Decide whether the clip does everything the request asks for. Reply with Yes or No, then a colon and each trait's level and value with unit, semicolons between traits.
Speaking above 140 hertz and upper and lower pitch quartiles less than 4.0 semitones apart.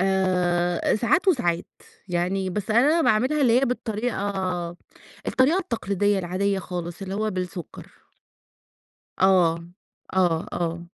No: high, 190 Hz; average, 4.4 semitones